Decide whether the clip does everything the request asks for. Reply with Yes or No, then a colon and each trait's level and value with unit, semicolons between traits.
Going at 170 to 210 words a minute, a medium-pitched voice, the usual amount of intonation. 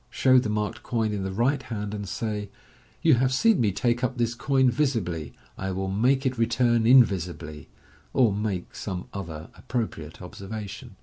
No: average, 175 wpm; low, 110 Hz; average, 4.6 semitones